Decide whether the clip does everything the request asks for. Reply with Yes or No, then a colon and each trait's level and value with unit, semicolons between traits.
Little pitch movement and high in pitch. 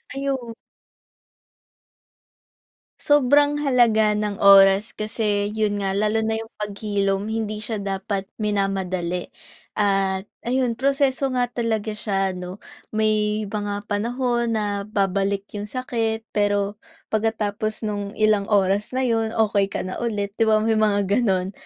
Yes: narrow, 2.1 semitones; high, 210 Hz